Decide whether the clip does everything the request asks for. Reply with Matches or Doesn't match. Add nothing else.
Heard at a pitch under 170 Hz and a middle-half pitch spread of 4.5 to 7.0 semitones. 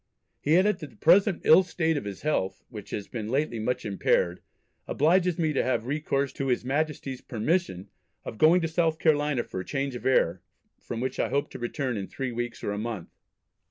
Matches